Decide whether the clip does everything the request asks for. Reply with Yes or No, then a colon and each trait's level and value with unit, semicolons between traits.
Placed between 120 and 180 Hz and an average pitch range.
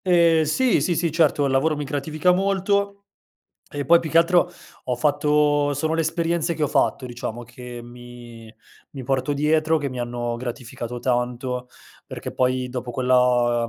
Yes: medium, 140 Hz; average, 4.7 semitones